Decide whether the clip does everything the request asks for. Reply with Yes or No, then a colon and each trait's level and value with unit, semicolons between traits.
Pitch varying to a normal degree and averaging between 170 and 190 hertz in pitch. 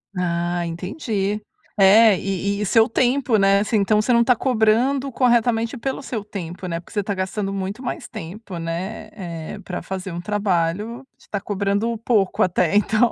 No: average, 3.4 semitones; high, 205 Hz